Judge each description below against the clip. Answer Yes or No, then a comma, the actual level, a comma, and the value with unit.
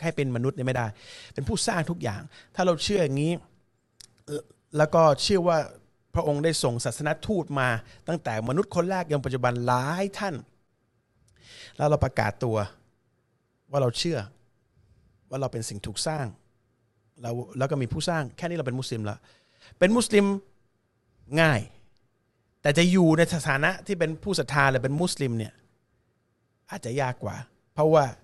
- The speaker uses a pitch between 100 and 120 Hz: No, low, 130 Hz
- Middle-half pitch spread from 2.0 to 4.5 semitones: No, average, 5.1 semitones